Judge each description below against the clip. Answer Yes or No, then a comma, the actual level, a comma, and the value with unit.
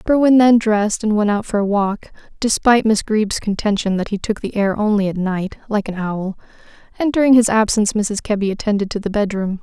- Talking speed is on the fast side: Yes, fast, 210 wpm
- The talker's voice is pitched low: No, high, 210 Hz